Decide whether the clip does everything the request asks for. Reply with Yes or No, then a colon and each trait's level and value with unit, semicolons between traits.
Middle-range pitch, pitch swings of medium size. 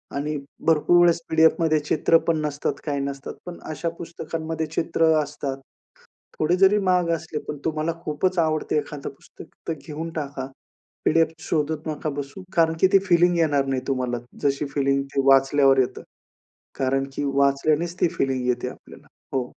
Yes: medium, 155 Hz; average, 3.1 semitones